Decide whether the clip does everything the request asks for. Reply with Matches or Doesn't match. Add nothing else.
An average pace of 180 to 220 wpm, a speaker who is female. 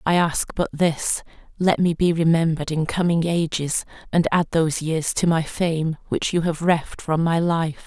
Matches